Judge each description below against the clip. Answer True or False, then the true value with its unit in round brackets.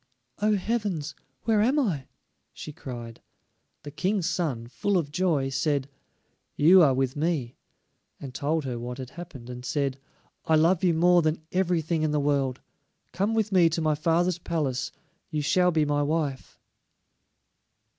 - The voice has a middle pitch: True (155 Hz)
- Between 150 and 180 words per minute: True (155 wpm)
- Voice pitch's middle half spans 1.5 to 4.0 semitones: False (4.4 semitones)